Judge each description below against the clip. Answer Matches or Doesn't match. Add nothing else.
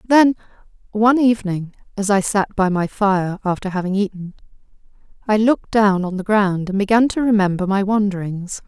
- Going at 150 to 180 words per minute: Matches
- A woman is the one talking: Matches